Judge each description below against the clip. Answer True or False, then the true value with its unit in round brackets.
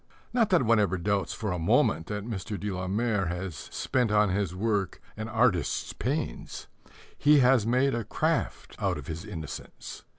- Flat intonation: False (3.9 semitones)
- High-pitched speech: False (105 Hz)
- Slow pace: False (175 wpm)